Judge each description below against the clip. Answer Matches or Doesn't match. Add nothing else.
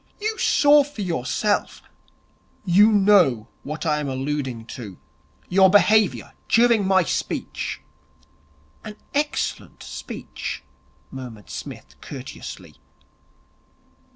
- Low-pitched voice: Doesn't match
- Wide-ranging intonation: Matches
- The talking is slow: Matches